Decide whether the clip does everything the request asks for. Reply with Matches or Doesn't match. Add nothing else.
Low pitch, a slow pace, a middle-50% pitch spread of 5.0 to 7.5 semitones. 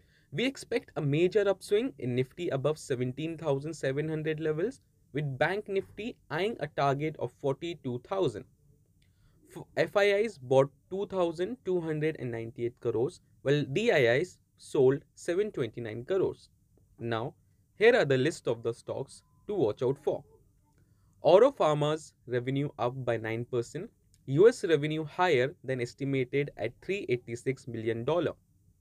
Doesn't match